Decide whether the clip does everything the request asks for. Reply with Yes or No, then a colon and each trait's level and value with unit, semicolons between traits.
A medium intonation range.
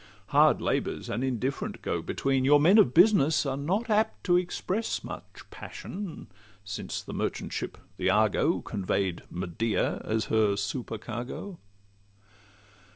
No: wide, 8.5 semitones